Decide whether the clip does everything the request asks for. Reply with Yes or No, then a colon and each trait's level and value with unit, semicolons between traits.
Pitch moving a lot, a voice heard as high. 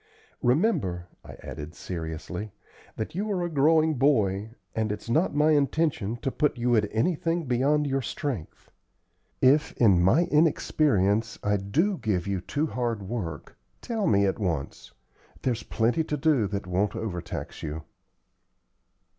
No: wide, 7.2 semitones; low, 120 Hz